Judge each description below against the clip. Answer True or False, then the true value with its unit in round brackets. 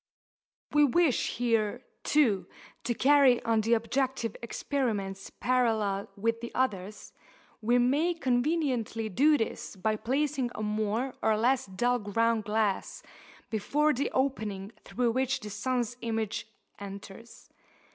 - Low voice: False (235 Hz)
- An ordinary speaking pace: False (125 wpm)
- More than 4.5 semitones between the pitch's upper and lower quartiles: False (3.5 semitones)